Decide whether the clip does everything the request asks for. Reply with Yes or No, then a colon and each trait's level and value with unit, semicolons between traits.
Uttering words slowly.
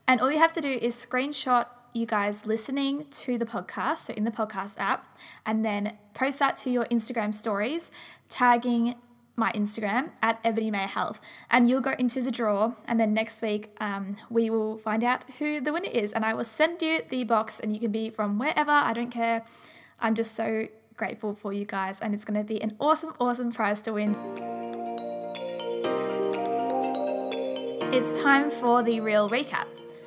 No: average, 185 wpm